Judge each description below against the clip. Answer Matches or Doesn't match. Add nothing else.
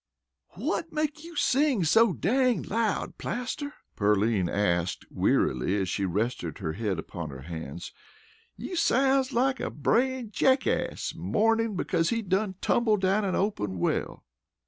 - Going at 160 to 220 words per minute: Doesn't match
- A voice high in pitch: Matches